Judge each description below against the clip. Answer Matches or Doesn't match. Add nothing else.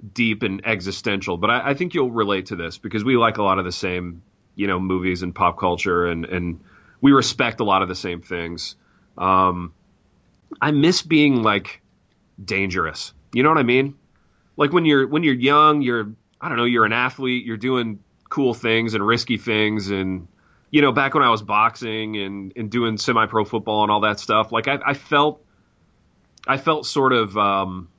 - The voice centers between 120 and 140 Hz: Doesn't match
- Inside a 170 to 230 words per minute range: Matches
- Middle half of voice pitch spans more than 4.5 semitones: Matches